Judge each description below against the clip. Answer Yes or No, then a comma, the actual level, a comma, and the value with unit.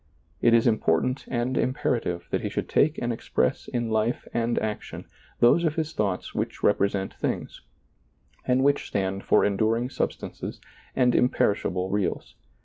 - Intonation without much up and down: No, average, 4.0 semitones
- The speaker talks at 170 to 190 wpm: No, average, 155 wpm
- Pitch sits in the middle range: No, low, 115 Hz